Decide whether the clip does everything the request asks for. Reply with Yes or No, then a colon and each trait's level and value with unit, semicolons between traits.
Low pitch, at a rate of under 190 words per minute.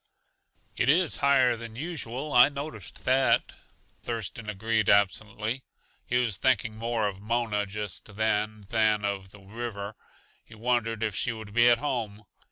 Yes: low, 110 Hz; average, 150 wpm